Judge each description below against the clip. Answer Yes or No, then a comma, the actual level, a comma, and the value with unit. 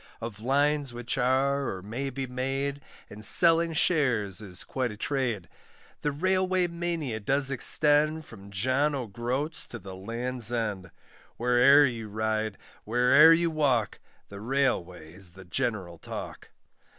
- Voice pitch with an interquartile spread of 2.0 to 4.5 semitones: No, average, 5.0 semitones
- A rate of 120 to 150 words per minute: Yes, average, 140 wpm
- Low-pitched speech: Yes, low, 125 Hz